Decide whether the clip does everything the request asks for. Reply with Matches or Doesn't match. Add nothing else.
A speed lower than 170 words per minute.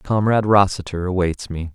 Matches